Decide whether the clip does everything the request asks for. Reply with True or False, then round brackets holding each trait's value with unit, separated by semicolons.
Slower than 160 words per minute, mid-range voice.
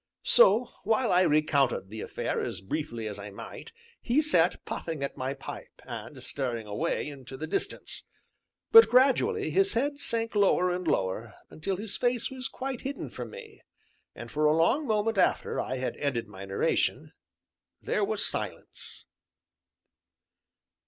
True (150 wpm; 165 Hz)